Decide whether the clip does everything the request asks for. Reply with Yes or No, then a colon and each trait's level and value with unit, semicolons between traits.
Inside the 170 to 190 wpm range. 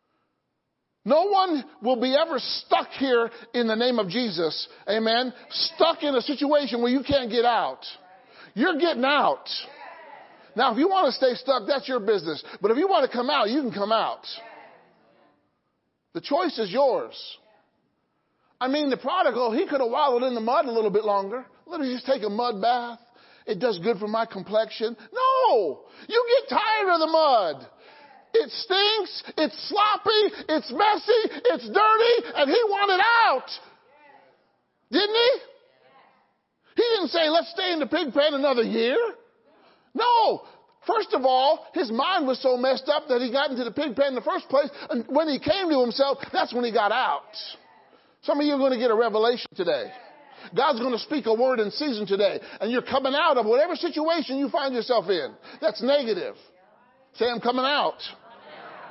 Yes: average, 180 wpm